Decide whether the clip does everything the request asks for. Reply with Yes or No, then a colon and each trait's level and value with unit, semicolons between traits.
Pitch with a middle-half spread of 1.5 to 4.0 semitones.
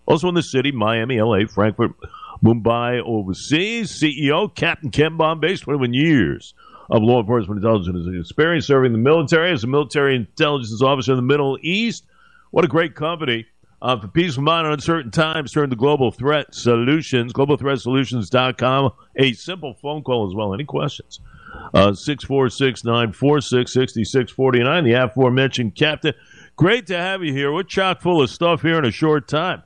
No: average, 4.4 semitones